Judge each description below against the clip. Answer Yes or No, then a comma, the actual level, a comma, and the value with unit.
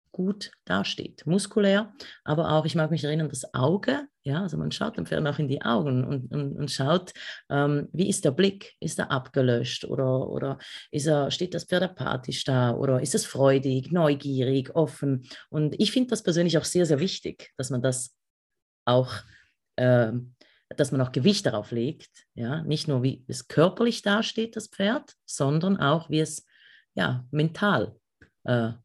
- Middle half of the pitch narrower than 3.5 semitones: No, wide, 5.6 semitones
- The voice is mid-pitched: Yes, medium, 150 Hz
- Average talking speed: Yes, average, 175 wpm